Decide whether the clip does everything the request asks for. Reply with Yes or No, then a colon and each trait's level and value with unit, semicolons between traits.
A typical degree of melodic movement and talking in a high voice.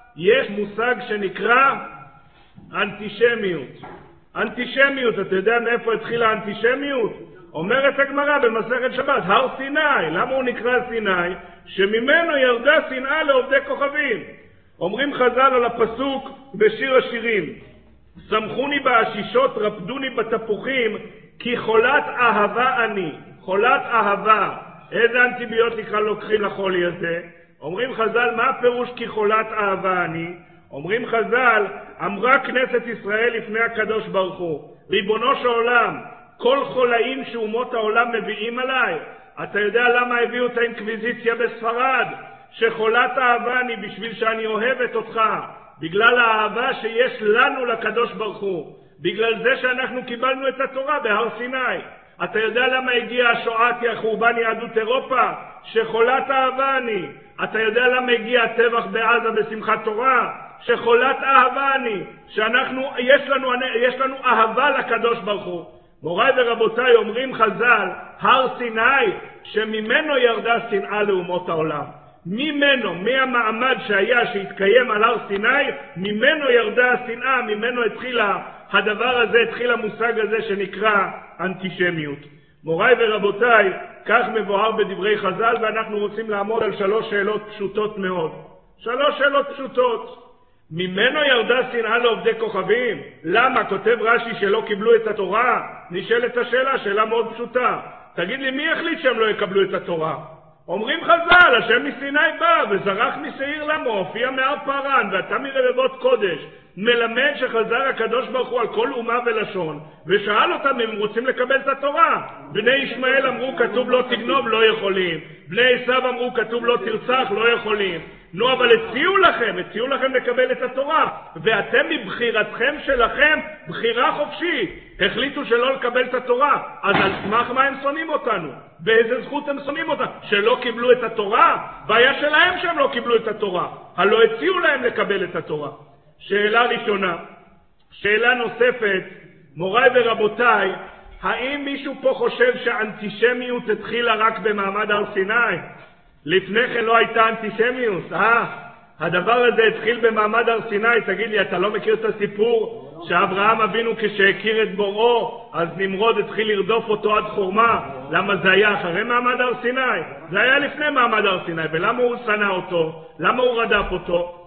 Yes: average, 3.6 semitones; high, 235 Hz